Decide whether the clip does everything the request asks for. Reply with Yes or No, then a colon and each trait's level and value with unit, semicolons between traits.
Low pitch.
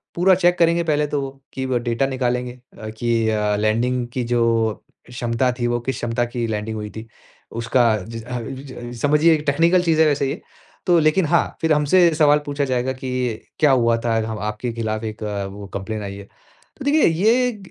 Yes: low, 125 Hz